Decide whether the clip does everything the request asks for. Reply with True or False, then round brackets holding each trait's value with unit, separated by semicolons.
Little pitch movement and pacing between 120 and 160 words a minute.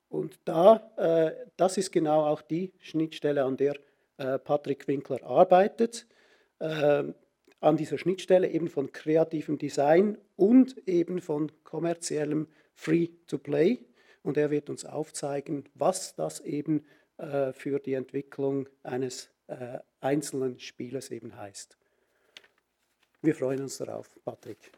False (3.2 semitones; 125 wpm)